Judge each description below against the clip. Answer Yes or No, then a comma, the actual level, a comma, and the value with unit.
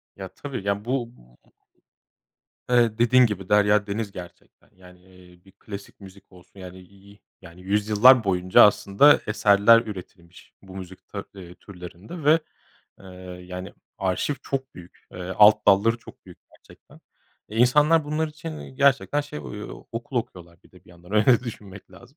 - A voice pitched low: Yes, low, 100 Hz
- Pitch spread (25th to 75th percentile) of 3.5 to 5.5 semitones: Yes, average, 4.5 semitones